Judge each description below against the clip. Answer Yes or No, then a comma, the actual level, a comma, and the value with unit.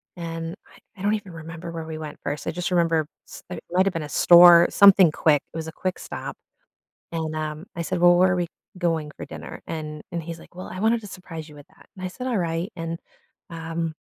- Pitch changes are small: Yes, narrow, 2.1 semitones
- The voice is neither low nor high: Yes, medium, 170 Hz